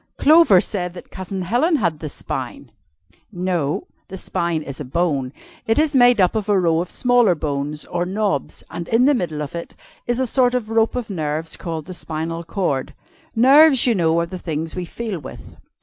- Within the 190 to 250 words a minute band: Yes, average, 195 wpm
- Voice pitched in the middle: Yes, medium, 180 Hz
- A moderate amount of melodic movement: No, wide, 6.0 semitones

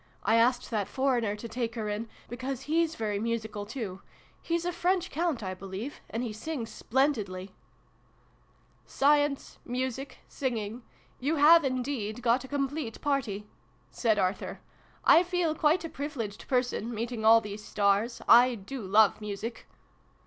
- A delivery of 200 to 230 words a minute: No, average, 160 wpm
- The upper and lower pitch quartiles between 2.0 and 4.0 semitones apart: No, average, 4.9 semitones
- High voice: Yes, high, 240 Hz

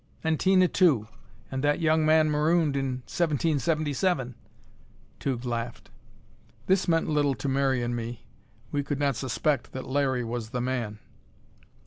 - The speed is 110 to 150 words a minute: Yes, average, 140 wpm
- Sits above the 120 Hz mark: Yes, medium, 140 Hz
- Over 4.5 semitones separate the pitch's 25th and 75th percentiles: No, average, 4.0 semitones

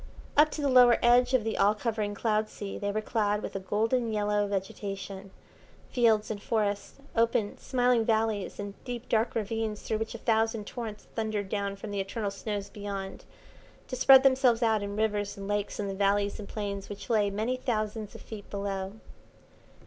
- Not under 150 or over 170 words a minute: No, average, 185 wpm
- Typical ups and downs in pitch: No, narrow, 2.1 semitones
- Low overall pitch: No, high, 215 Hz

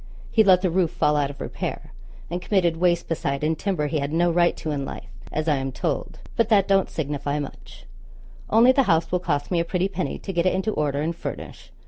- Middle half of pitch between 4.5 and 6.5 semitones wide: No, average, 4.0 semitones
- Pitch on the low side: No, medium, 170 Hz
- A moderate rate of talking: No, fast, 230 wpm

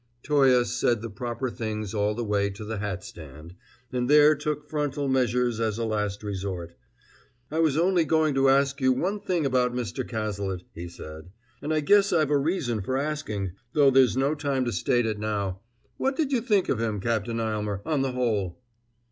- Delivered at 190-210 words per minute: Yes, average, 195 wpm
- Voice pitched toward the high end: No, low, 125 Hz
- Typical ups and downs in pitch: No, wide, 5.8 semitones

